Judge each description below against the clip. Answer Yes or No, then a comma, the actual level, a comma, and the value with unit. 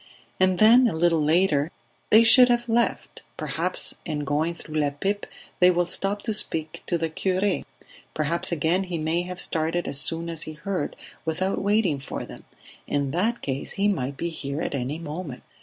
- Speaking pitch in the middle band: Yes, medium, 170 Hz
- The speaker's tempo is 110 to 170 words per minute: No, average, 185 wpm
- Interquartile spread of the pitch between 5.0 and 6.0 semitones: No, average, 4.2 semitones